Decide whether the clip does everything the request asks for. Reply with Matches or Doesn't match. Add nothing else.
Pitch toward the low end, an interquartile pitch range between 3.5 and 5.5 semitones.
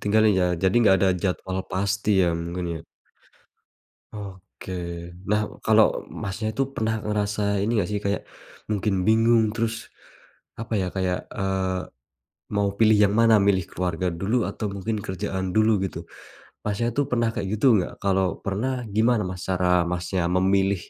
Doesn't match